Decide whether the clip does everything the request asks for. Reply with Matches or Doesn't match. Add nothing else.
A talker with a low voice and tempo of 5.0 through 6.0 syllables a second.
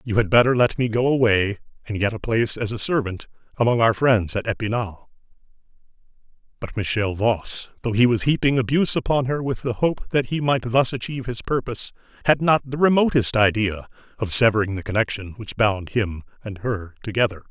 Matches